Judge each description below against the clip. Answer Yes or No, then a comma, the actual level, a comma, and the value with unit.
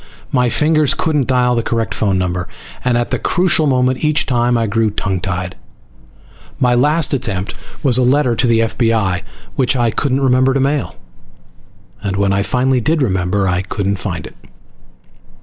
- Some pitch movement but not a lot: Yes, average, 5.0 semitones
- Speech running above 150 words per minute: Yes, average, 170 wpm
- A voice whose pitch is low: Yes, low, 120 Hz